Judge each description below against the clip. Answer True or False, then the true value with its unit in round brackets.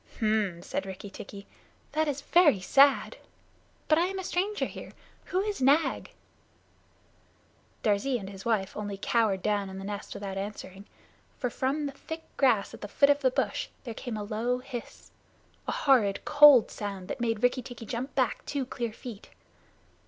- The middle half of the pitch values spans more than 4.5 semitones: True (5.5 semitones)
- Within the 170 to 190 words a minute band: True (175 wpm)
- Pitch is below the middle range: False (235 Hz)